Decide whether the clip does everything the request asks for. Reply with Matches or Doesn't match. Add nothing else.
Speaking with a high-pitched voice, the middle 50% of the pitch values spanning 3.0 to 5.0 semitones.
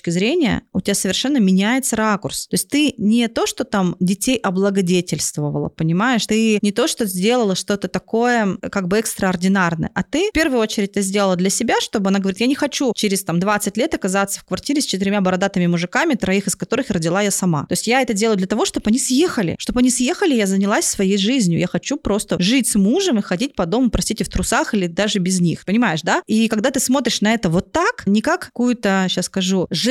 Matches